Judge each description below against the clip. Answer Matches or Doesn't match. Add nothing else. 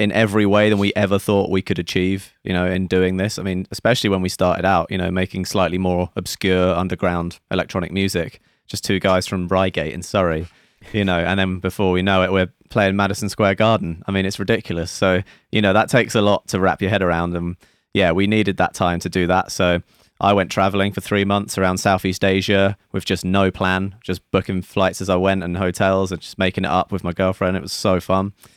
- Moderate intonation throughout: Doesn't match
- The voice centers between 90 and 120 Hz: Matches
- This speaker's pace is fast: Matches